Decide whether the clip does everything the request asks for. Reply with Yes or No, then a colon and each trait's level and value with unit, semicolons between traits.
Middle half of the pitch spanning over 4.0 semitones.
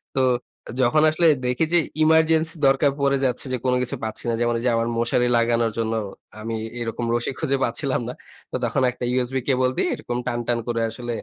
No: average, 2.7 semitones